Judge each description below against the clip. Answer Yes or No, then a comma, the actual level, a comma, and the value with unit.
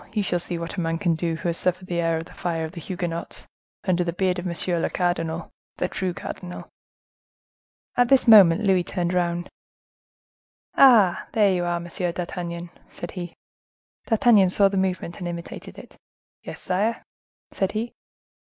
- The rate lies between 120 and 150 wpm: No, average, 170 wpm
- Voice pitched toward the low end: No, medium, 175 Hz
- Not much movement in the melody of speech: Yes, narrow, 1.9 semitones